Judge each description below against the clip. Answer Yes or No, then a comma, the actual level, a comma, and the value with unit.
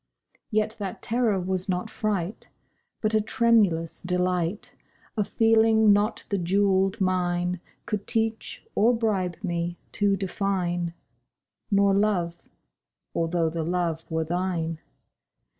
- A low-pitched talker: No, high, 190 Hz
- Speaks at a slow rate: Yes, slow, 110 wpm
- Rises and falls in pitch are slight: No, average, 3.4 semitones